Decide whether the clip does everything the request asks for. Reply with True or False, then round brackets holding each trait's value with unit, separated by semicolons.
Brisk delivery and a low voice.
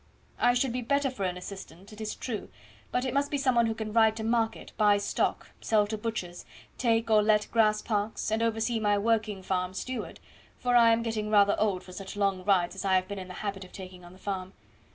False (235 wpm; 215 Hz)